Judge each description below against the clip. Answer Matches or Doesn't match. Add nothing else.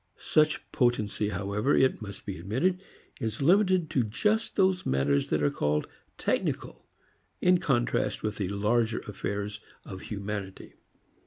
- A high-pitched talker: Doesn't match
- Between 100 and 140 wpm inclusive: Matches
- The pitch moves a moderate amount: Doesn't match